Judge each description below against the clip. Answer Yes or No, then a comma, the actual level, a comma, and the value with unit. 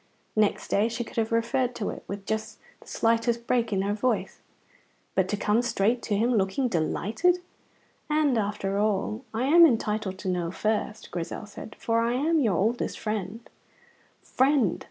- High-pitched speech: Yes, high, 220 Hz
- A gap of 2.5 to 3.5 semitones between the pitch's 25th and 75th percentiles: Yes, average, 2.9 semitones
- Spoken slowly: No, average, 170 wpm